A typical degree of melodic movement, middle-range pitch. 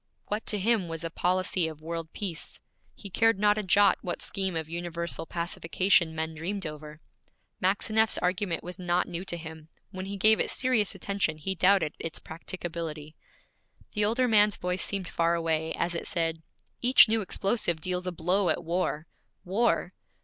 Yes: average, 3.5 semitones; medium, 180 Hz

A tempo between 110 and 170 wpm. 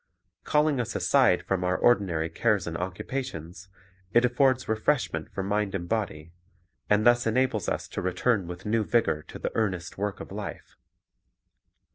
Yes: average, 155 wpm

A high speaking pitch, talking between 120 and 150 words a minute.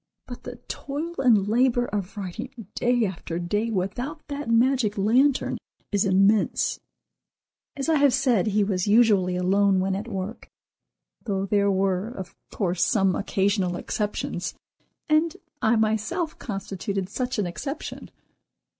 Yes: high, 210 Hz; slow, 135 wpm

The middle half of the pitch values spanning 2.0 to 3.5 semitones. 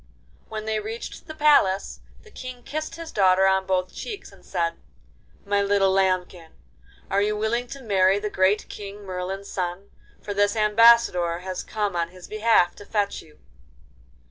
Yes: average, 2.8 semitones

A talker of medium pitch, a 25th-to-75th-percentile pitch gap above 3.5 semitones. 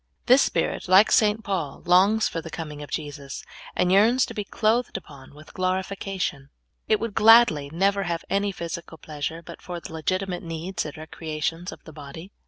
Yes: medium, 175 Hz; average, 4.1 semitones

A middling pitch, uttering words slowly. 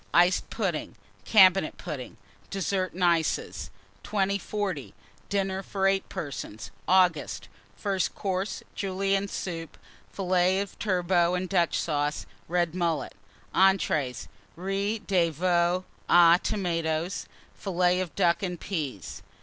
Yes: medium, 180 Hz; slow, 110 wpm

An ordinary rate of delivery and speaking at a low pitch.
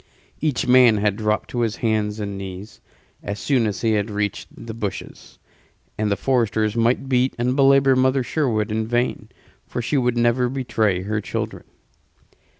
Yes: average, 165 wpm; low, 115 Hz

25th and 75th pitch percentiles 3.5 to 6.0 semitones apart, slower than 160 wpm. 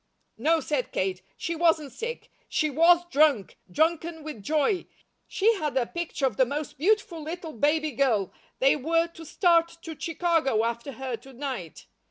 No: average, 4.1 semitones; average, 165 wpm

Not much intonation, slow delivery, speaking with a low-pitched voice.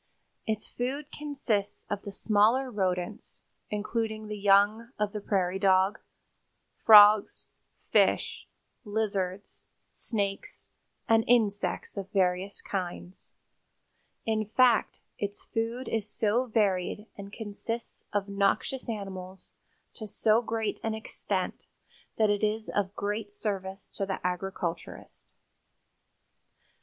No: narrow, 2.1 semitones; slow, 110 wpm; high, 205 Hz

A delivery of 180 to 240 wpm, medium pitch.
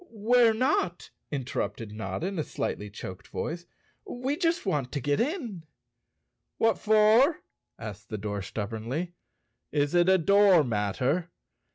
No: slow, 135 wpm; medium, 170 Hz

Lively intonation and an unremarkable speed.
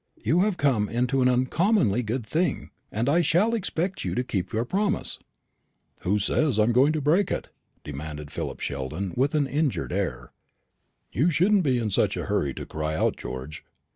Yes: wide, 7.8 semitones; average, 185 wpm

